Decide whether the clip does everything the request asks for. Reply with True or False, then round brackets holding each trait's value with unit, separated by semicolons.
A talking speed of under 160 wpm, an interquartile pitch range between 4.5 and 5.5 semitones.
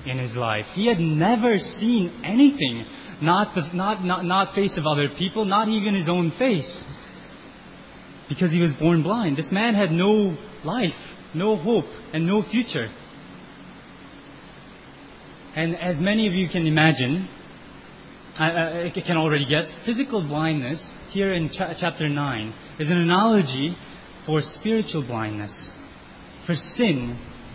True (140 wpm; 5.0 semitones)